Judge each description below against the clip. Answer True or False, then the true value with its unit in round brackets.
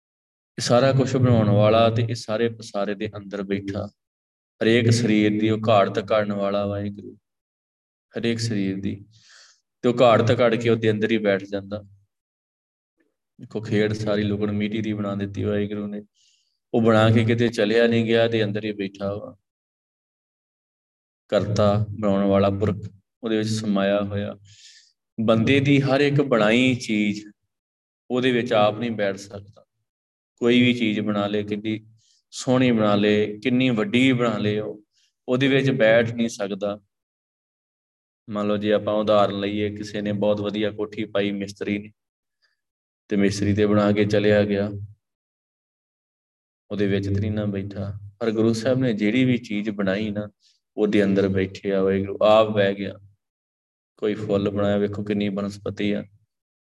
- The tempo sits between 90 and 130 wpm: False (150 wpm)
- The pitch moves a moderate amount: False (1.9 semitones)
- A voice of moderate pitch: False (105 Hz)